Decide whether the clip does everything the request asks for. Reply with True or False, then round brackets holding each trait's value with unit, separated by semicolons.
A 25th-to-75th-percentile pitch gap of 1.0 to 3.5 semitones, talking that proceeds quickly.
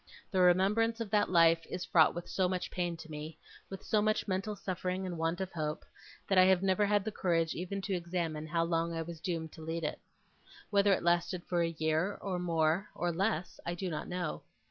True (2.5 semitones; 220 wpm)